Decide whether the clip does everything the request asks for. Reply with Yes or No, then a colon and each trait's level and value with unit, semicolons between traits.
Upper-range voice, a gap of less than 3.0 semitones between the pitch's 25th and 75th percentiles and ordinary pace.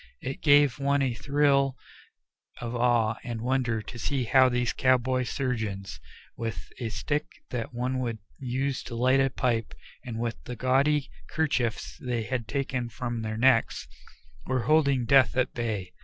No: low, 125 Hz; narrow, 2.6 semitones; average, 155 wpm